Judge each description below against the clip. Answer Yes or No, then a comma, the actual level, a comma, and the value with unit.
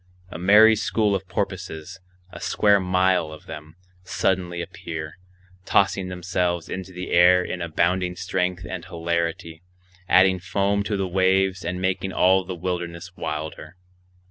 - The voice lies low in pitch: Yes, very low, 90 Hz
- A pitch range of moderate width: No, narrow, 1.7 semitones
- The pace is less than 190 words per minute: Yes, average, 140 wpm